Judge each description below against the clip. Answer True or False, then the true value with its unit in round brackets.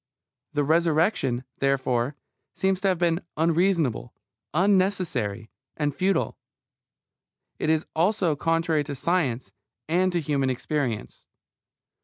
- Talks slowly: True (105 wpm)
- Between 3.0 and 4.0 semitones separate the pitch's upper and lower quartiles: False (4.5 semitones)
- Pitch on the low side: False (160 Hz)